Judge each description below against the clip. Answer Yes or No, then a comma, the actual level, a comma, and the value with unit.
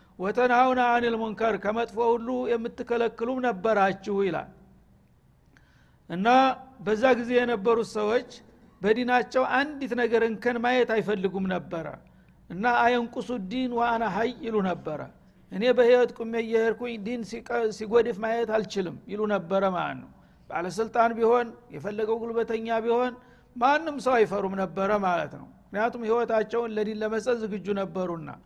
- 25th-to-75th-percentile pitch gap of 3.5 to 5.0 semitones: No, narrow, 2.6 semitones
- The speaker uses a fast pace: Yes, fast, 120 wpm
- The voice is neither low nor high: No, high, 230 Hz